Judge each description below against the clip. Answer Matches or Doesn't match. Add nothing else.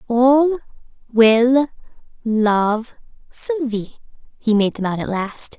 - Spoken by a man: Doesn't match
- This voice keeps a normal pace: Doesn't match